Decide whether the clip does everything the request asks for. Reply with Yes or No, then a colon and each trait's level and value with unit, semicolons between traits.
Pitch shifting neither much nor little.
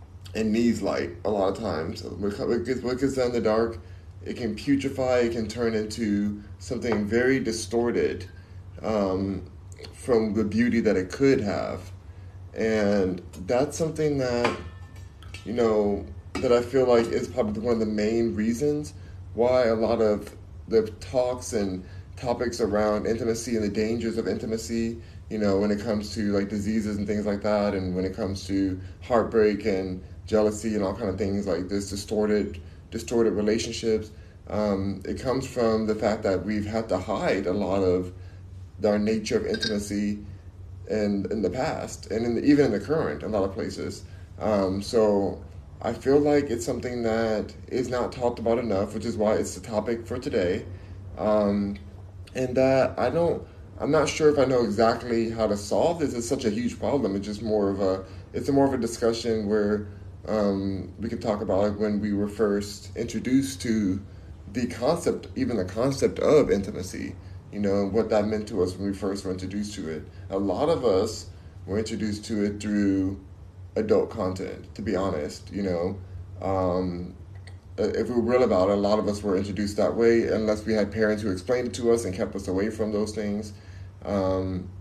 Yes: average, 3.2 semitones